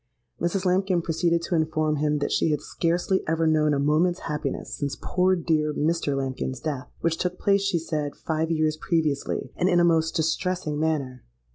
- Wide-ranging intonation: No, narrow, 2.4 semitones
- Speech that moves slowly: No, average, 180 wpm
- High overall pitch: No, medium, 160 Hz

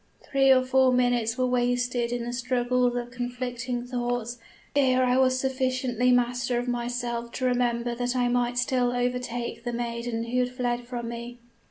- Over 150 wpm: Yes, average, 170 wpm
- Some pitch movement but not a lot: No, narrow, 0.8 semitones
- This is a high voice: Yes, high, 245 Hz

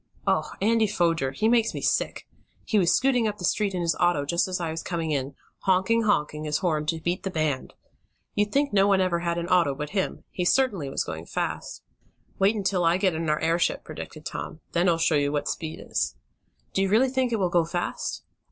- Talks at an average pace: No, fast, 225 wpm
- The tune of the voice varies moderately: Yes, average, 4.2 semitones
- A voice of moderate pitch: Yes, medium, 175 Hz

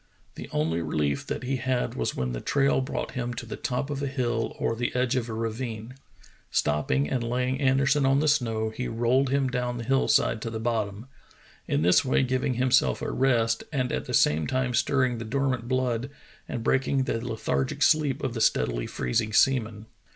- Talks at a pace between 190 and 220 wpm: Yes, fast, 205 wpm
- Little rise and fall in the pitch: No, average, 3.0 semitones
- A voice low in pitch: Yes, low, 120 Hz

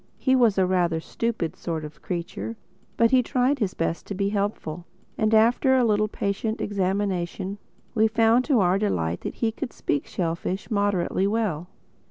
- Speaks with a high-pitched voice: Yes, high, 200 Hz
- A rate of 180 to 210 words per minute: No, average, 170 wpm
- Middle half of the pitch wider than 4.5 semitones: No, average, 4.1 semitones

